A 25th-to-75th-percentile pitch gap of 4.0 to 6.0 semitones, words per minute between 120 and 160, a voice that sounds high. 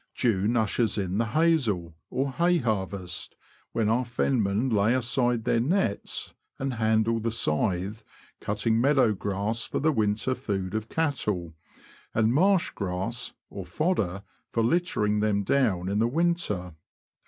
No: average, 4.3 semitones; average, 140 wpm; low, 110 Hz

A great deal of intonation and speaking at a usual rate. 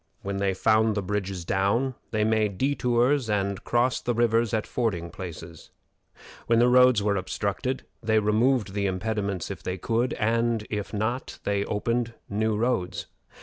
No: average, 3.0 semitones; average, 155 wpm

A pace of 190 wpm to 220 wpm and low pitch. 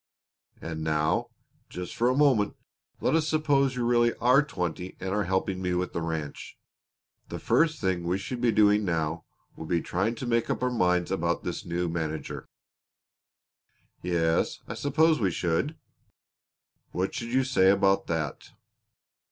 No: average, 160 wpm; very low, 95 Hz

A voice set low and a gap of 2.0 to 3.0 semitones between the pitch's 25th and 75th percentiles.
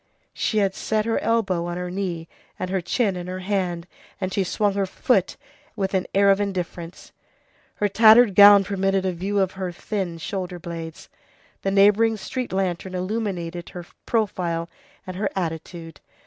No: high, 190 Hz; narrow, 2.4 semitones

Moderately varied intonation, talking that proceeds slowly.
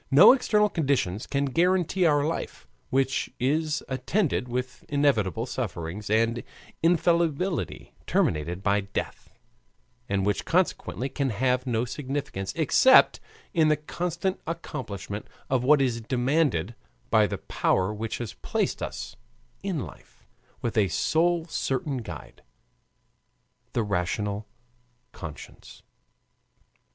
No: wide, 6.8 semitones; slow, 115 wpm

